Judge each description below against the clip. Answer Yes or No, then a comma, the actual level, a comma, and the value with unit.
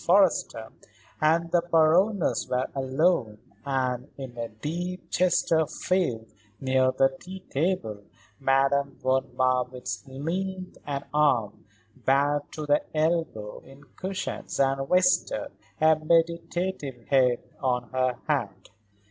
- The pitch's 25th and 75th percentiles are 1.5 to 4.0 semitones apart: No, average, 4.6 semitones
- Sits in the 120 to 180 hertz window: Yes, medium, 140 Hz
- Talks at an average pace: No, slow, 110 wpm